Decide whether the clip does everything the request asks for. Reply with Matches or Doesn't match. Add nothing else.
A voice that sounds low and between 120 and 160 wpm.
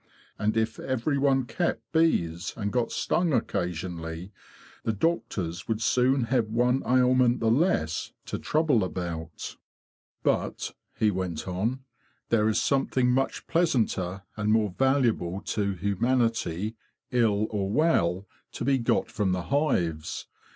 Matches